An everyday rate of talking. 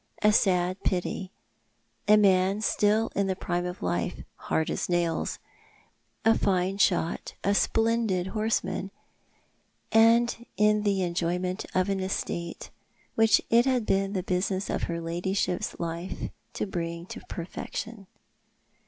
Yes: average, 150 wpm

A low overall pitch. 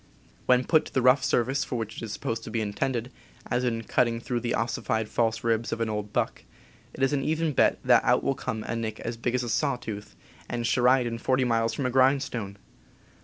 Yes: low, 120 Hz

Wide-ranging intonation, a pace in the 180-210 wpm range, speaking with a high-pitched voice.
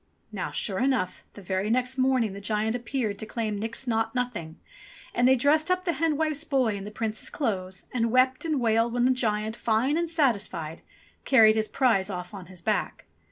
No: average, 4.0 semitones; average, 200 wpm; high, 230 Hz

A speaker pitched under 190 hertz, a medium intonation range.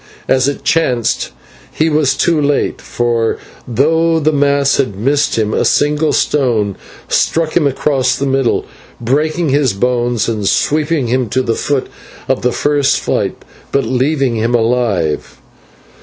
Yes: low, 135 Hz; average, 3.7 semitones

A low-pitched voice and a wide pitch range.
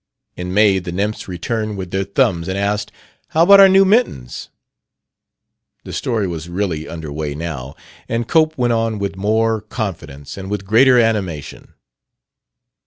No: low, 100 Hz; average, 4.6 semitones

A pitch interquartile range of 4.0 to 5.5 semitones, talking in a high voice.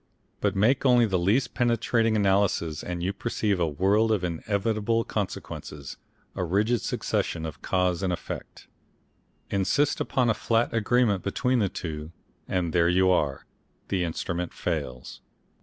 No: average, 4.6 semitones; very low, 95 Hz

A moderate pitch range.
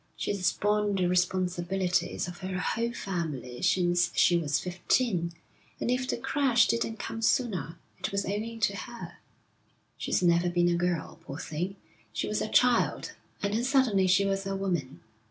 Yes: average, 3.7 semitones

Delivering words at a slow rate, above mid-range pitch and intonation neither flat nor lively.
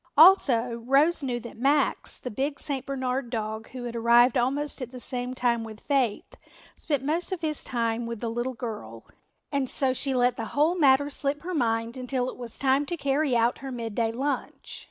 No: average, 195 wpm; very high, 255 Hz; average, 3.1 semitones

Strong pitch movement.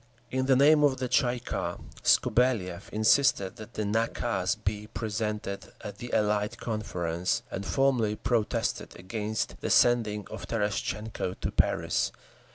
No: average, 2.9 semitones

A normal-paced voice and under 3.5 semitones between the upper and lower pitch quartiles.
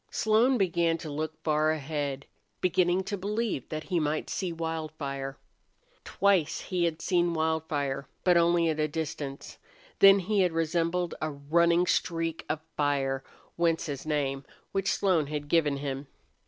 Yes: average, 150 wpm; average, 3.0 semitones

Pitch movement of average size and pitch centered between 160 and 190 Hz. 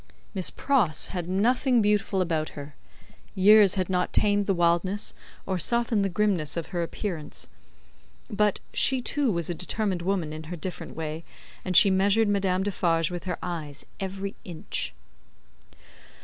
Yes: average, 3.3 semitones; medium, 185 Hz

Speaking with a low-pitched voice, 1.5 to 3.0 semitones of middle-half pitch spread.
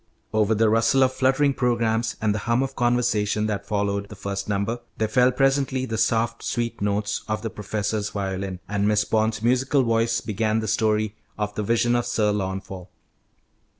Yes: low, 110 Hz; narrow, 2.5 semitones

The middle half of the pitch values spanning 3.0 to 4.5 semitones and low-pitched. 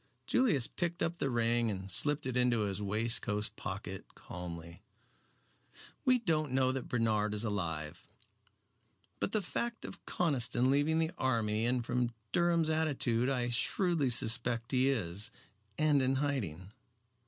No: wide, 5.6 semitones; low, 125 Hz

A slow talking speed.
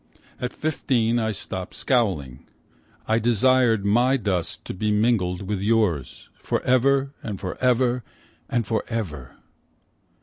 Yes: slow, 110 wpm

